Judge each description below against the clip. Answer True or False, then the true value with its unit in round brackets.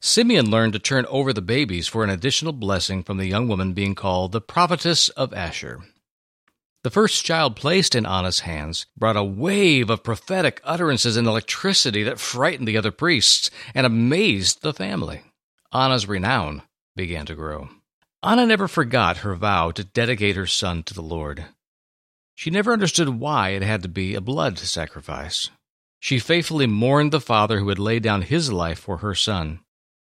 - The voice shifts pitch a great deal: True (6.7 semitones)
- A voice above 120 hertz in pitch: False (110 Hz)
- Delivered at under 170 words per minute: False (175 wpm)